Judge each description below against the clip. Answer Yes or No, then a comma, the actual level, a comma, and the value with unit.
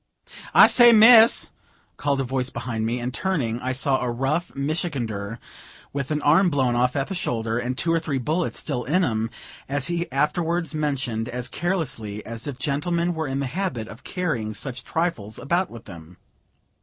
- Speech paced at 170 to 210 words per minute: Yes, average, 180 wpm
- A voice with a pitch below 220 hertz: Yes, low, 135 Hz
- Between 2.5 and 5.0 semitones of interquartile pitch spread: No, wide, 5.6 semitones